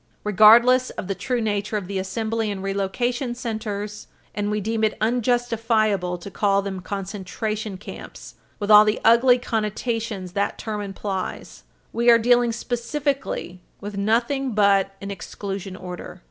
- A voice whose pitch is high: Yes, high, 215 Hz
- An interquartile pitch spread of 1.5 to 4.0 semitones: Yes, average, 2.9 semitones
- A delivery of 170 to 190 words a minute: No, average, 145 wpm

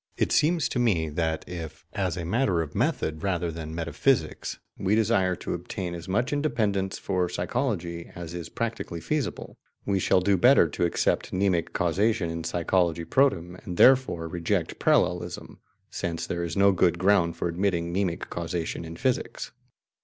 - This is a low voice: Yes, very low, 90 Hz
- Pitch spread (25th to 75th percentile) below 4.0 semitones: Yes, average, 3.3 semitones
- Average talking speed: Yes, average, 160 wpm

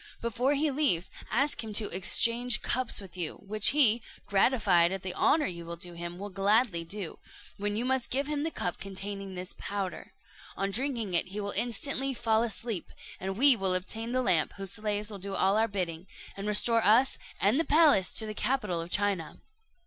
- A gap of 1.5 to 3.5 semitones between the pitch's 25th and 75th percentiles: No, average, 4.3 semitones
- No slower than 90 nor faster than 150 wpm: No, average, 195 wpm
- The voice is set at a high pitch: Yes, high, 205 Hz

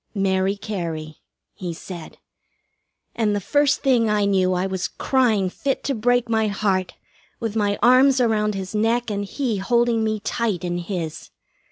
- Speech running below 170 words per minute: Yes, average, 160 wpm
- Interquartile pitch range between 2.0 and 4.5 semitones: Yes, average, 3.8 semitones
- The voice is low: No, high, 210 Hz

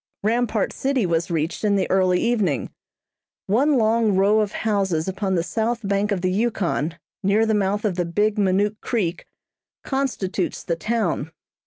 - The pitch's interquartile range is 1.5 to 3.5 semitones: Yes, average, 3.2 semitones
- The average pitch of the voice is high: Yes, high, 200 Hz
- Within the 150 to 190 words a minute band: Yes, average, 160 wpm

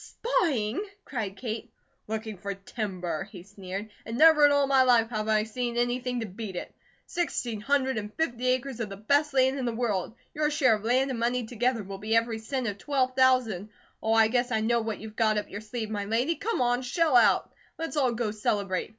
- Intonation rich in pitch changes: No, average, 3.3 semitones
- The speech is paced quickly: Yes, fast, 215 wpm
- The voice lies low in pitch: No, high, 230 Hz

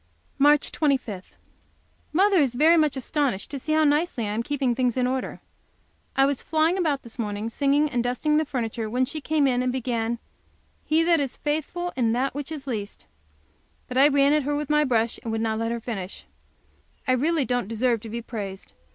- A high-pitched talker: Yes, very high, 260 Hz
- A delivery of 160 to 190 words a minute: No, fast, 205 wpm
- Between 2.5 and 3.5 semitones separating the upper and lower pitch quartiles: No, average, 4.3 semitones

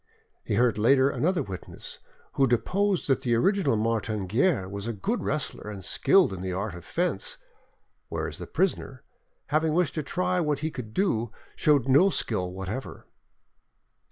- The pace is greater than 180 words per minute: No, average, 160 wpm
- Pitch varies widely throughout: Yes, wide, 8.0 semitones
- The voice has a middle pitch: No, low, 130 Hz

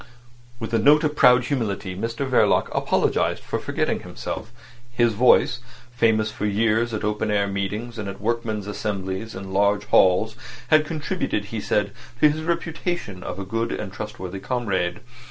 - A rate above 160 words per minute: No, average, 155 wpm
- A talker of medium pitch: No, low, 110 Hz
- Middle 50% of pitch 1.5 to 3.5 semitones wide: Yes, average, 3.2 semitones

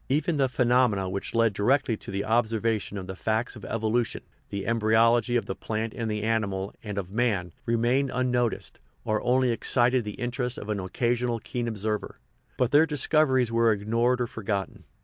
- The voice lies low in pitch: Yes, low, 115 Hz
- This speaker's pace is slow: No, average, 185 wpm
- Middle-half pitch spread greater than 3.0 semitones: No, narrow, 2.6 semitones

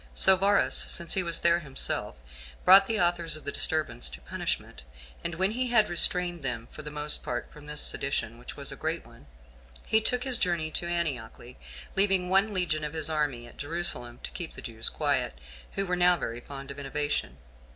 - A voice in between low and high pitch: Yes, medium, 160 Hz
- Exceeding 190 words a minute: Yes, average, 200 wpm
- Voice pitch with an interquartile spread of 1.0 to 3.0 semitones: No, average, 4.6 semitones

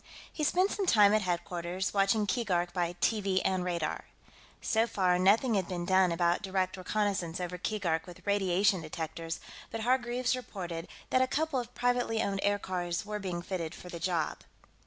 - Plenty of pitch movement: No, average, 3.8 semitones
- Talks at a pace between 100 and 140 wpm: No, average, 170 wpm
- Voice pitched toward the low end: No, high, 190 Hz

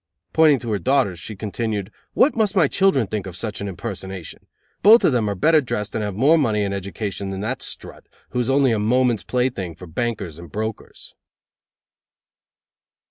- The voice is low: Yes, low, 110 Hz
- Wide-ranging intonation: No, average, 4.8 semitones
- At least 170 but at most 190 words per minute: Yes, average, 185 wpm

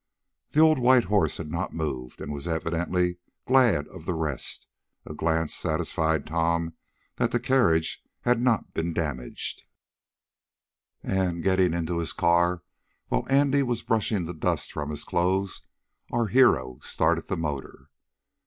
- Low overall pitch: Yes, very low, 85 Hz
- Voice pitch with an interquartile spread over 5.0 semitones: Yes, wide, 5.4 semitones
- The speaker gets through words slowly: No, average, 145 wpm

